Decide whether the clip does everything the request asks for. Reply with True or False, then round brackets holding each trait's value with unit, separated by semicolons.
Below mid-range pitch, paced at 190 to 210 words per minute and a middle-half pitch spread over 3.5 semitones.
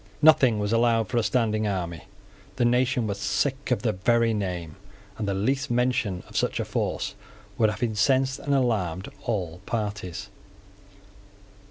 False (110 Hz; 155 wpm; 3.9 semitones)